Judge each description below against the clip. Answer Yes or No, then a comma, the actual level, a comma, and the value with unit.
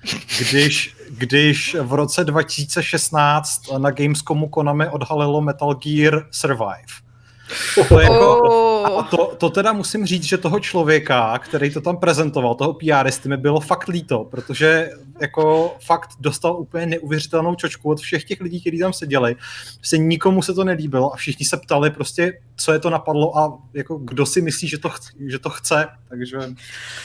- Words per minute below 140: No, average, 165 wpm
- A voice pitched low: No, medium, 155 Hz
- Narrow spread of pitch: No, average, 3.2 semitones